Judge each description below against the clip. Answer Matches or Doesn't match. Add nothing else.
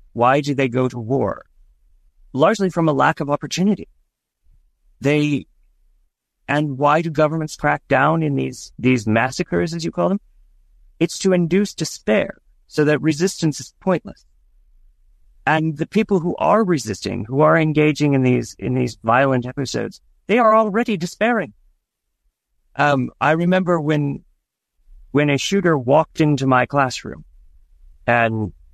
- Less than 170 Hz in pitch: Matches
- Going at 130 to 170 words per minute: Matches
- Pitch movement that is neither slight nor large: Doesn't match